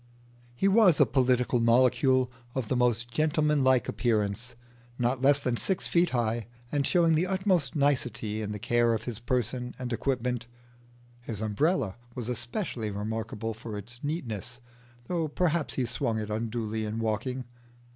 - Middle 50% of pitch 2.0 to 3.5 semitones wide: No, average, 3.9 semitones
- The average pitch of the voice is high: No, low, 125 Hz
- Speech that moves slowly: No, average, 155 wpm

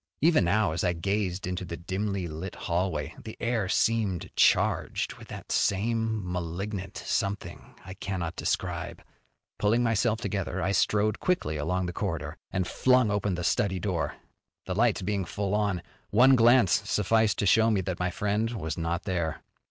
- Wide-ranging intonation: No, average, 3.4 semitones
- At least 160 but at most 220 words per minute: Yes, average, 165 wpm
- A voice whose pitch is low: Yes, very low, 95 Hz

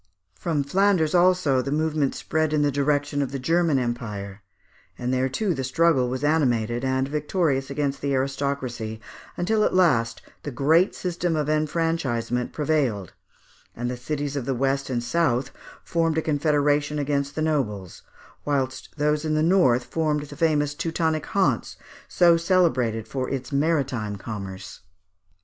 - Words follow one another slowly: No, average, 150 wpm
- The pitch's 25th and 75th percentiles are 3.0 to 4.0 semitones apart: Yes, average, 3.7 semitones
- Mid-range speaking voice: Yes, medium, 145 Hz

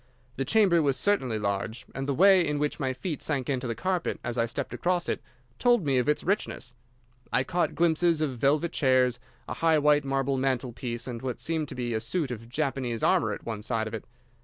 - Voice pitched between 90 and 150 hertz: Yes, low, 135 Hz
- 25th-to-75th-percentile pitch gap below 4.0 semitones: No, average, 4.8 semitones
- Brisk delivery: Yes, fast, 220 wpm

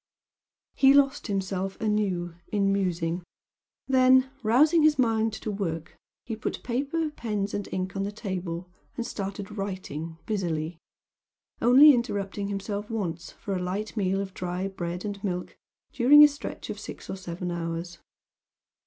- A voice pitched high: Yes, high, 200 Hz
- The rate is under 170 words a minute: Yes, average, 145 wpm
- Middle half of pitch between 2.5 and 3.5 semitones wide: No, average, 4.2 semitones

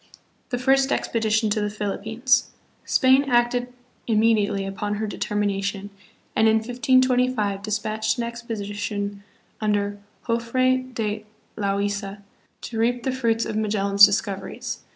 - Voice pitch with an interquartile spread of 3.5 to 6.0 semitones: No, average, 3.0 semitones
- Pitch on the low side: No, high, 220 Hz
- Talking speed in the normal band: No, slow, 120 wpm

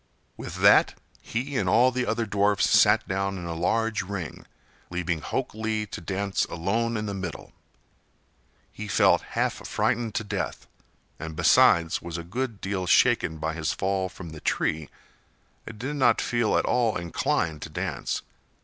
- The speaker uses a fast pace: No, average, 165 wpm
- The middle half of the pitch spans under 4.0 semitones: No, average, 4.5 semitones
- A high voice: No, low, 100 Hz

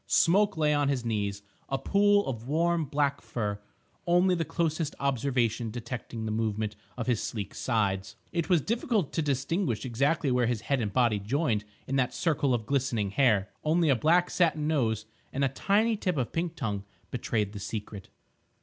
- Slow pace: No, average, 175 wpm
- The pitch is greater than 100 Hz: Yes, low, 135 Hz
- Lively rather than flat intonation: Yes, wide, 6.5 semitones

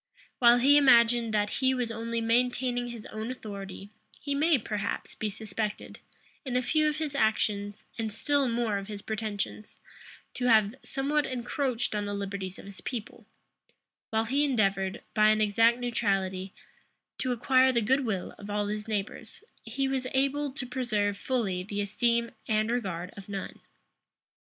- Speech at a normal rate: Yes, average, 160 wpm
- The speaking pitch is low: No, high, 225 Hz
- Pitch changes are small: No, average, 3.6 semitones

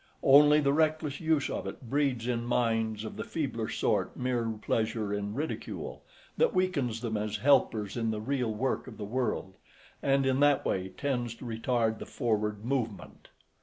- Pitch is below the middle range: Yes, low, 120 Hz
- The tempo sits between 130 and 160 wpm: No, average, 170 wpm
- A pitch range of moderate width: Yes, average, 4.1 semitones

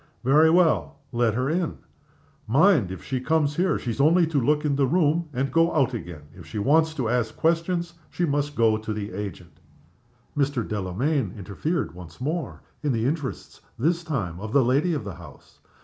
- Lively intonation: Yes, wide, 6.5 semitones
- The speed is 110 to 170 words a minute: No, average, 185 wpm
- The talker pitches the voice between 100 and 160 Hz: Yes, medium, 140 Hz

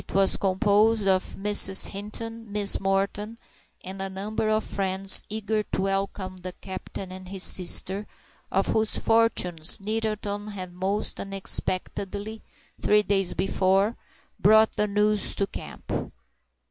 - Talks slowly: Yes, slow, 130 wpm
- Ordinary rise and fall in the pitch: No, narrow, 1.8 semitones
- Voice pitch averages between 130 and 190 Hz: No, high, 200 Hz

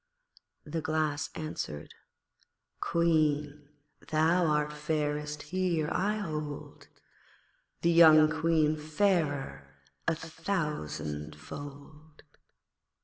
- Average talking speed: No, slow, 75 wpm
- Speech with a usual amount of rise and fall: No, narrow, 1.9 semitones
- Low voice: No, medium, 155 Hz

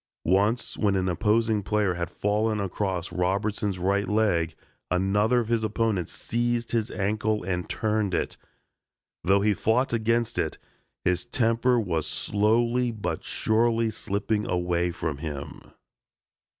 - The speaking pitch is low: Yes, low, 105 Hz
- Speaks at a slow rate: Yes, slow, 130 wpm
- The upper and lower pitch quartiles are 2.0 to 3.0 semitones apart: No, average, 3.4 semitones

